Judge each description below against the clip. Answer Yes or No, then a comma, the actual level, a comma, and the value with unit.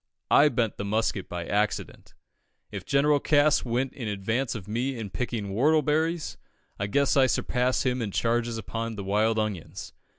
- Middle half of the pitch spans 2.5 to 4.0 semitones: No, average, 4.4 semitones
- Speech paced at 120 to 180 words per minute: Yes, average, 165 wpm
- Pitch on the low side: Yes, low, 115 Hz